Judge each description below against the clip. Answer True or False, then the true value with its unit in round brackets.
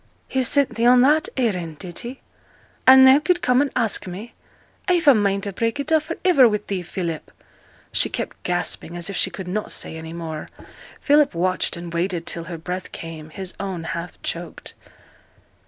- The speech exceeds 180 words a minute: True (190 wpm)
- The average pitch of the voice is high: True (195 Hz)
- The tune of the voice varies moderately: False (7.3 semitones)